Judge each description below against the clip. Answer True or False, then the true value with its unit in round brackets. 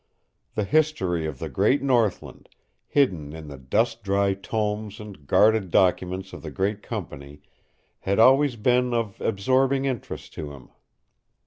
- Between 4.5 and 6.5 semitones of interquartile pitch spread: True (5.1 semitones)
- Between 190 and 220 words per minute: False (140 wpm)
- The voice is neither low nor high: False (105 Hz)